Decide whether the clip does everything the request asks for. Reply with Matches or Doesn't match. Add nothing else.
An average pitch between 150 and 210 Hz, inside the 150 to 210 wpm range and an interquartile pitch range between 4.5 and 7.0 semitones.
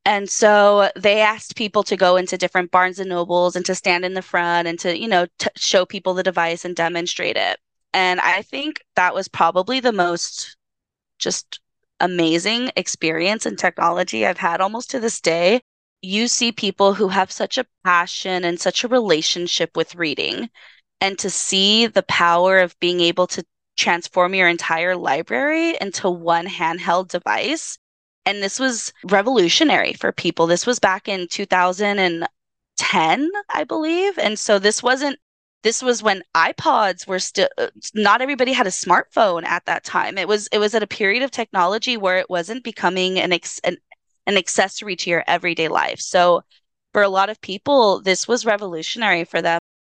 Doesn't match